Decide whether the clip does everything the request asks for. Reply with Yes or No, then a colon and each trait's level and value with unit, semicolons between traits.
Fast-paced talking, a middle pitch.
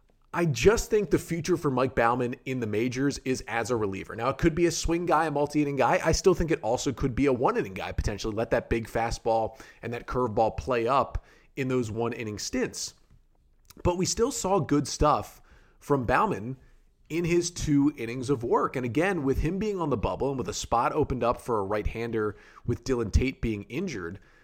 No: fast, 220 wpm; low, 130 Hz